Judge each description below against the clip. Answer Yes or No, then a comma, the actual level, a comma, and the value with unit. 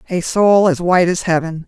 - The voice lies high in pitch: No, medium, 175 Hz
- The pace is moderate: No, fast, 215 wpm